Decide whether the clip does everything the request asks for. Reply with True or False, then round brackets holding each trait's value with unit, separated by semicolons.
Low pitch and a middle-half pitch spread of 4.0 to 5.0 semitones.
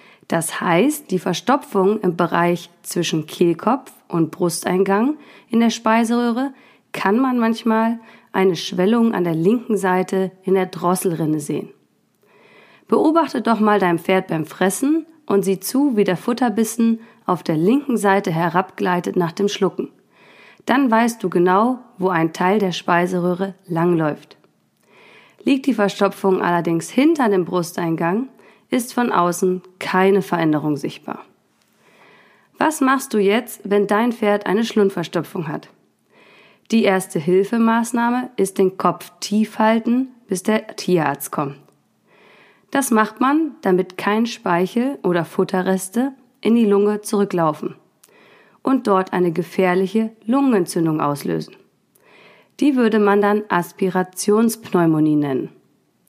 False (195 Hz; 4.3 semitones)